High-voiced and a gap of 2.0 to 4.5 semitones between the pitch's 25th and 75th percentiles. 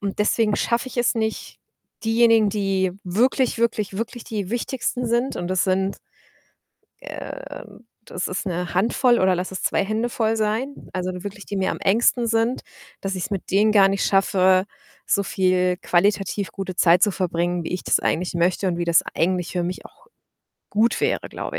Yes: high, 195 Hz; average, 3.6 semitones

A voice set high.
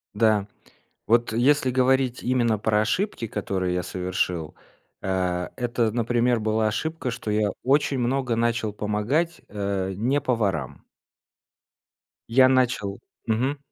No: low, 115 Hz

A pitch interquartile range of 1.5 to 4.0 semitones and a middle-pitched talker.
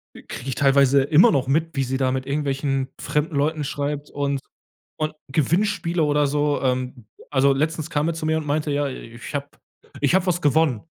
Yes: narrow, 2.4 semitones; medium, 145 Hz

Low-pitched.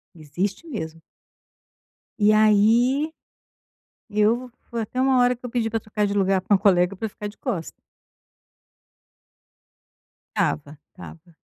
No: high, 210 Hz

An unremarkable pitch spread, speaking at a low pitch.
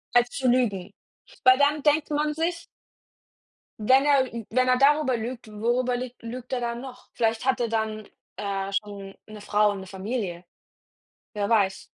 No: average, 3.6 semitones; high, 235 Hz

